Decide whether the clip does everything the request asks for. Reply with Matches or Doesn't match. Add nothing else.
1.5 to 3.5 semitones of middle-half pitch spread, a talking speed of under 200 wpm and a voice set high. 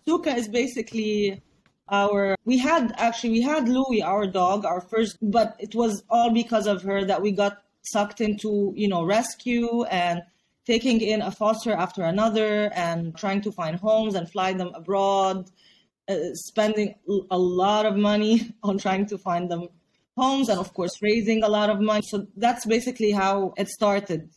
Matches